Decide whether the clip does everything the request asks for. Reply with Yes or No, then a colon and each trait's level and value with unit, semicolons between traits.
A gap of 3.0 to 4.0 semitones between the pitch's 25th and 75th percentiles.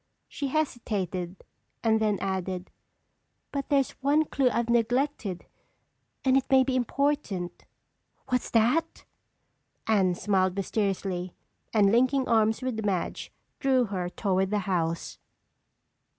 No: wide, 5.5 semitones